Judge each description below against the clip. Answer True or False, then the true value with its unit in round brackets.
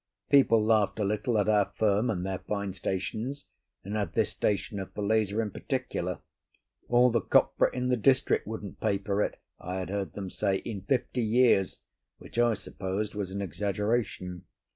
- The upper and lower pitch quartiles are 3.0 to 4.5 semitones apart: False (2.5 semitones)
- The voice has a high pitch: False (105 Hz)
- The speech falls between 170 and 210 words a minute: True (175 wpm)